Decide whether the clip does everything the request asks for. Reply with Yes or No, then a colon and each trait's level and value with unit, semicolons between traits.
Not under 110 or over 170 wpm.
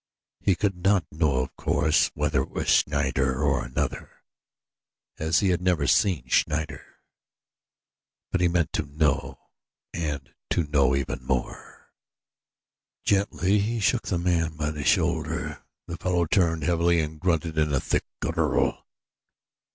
Yes: average, 140 wpm